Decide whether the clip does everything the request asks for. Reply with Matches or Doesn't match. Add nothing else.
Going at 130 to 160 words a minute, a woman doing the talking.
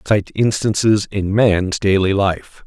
Doesn't match